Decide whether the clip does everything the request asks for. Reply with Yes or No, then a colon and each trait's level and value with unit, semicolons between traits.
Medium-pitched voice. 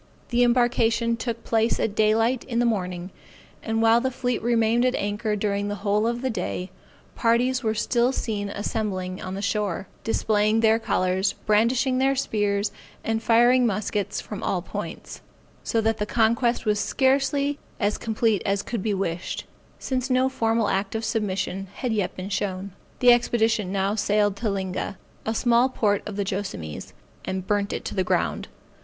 No: high, 220 Hz